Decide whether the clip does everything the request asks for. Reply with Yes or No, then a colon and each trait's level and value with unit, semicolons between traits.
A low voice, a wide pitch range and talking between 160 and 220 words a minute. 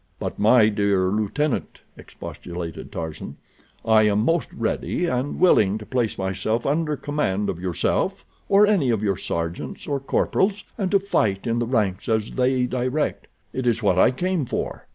Yes: low, 115 Hz; wide, 6.2 semitones; average, 165 wpm